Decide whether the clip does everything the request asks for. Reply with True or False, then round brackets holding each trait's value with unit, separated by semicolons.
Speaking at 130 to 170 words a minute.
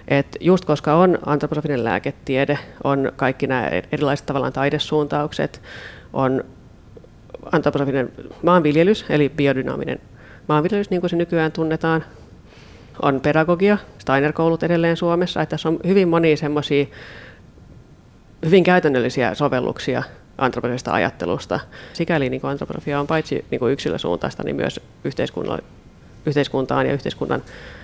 False (110 wpm)